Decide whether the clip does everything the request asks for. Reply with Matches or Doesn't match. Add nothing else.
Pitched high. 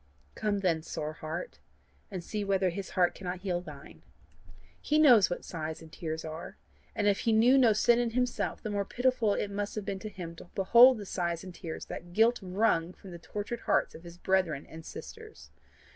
Matches